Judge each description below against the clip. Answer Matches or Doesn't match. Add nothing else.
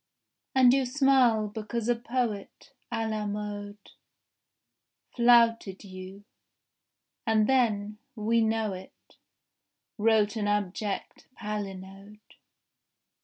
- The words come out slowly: Matches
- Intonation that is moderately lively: Doesn't match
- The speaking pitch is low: Doesn't match